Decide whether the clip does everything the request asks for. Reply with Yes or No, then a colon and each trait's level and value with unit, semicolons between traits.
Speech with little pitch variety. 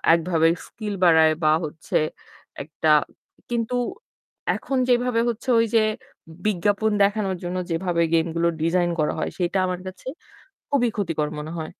No: average, 4.6 semitones